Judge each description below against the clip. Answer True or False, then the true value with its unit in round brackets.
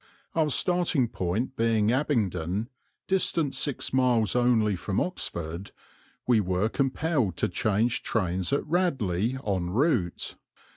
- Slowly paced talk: True (115 wpm)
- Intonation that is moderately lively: False (6.4 semitones)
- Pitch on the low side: True (115 Hz)